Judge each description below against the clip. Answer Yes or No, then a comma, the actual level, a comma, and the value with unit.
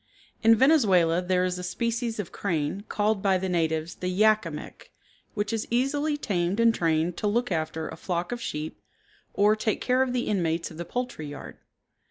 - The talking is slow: No, average, 195 wpm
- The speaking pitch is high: Yes, high, 195 Hz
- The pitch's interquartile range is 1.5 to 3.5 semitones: No, average, 5.1 semitones